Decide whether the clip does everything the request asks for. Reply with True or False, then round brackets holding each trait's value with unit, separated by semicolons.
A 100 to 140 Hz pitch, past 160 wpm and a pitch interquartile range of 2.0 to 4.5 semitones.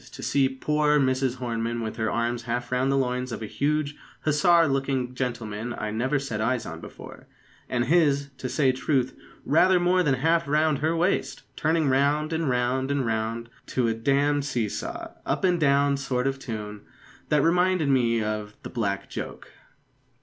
True (135 Hz; 180 wpm; 4.0 semitones)